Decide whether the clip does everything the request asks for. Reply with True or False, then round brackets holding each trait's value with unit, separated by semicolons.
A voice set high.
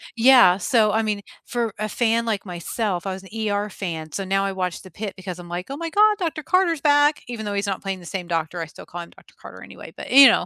True (205 Hz)